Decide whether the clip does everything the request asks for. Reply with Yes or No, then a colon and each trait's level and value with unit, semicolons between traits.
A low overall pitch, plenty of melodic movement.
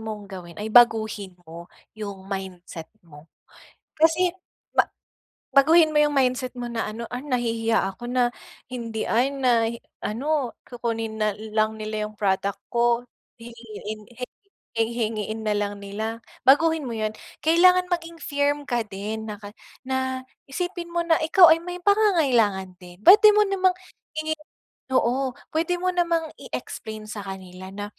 No: high, 235 Hz; wide, 6.3 semitones